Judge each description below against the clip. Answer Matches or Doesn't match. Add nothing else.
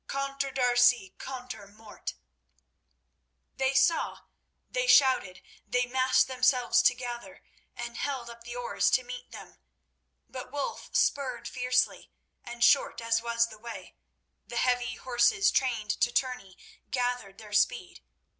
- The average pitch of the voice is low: Doesn't match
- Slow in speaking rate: Matches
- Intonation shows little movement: Matches